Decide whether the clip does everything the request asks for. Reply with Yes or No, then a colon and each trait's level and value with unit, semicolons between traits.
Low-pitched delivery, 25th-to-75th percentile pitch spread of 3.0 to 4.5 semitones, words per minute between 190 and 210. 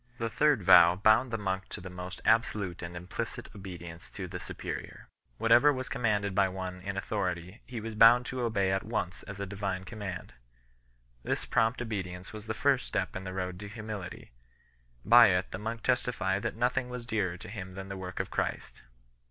Yes: low, 100 Hz; average, 3.6 semitones; average, 195 wpm